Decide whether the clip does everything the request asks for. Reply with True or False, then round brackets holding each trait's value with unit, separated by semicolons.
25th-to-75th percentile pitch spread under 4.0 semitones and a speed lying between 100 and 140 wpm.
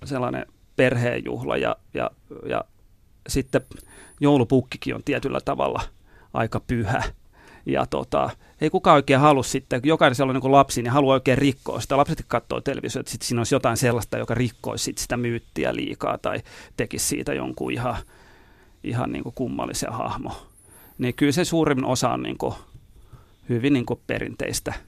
False (2.8 semitones; 155 wpm)